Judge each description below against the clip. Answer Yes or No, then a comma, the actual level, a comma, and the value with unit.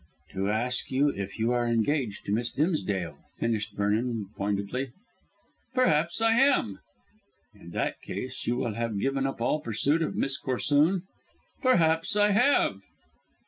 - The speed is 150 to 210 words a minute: No, average, 140 wpm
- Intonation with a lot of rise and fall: Yes, wide, 6.5 semitones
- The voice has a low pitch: Yes, low, 125 Hz